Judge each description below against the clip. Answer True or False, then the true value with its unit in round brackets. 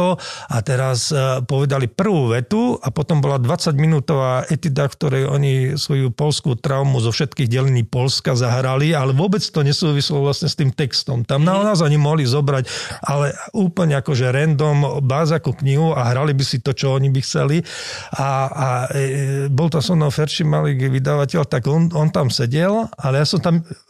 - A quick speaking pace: True (180 wpm)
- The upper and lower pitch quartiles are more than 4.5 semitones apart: False (2.8 semitones)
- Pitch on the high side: False (140 Hz)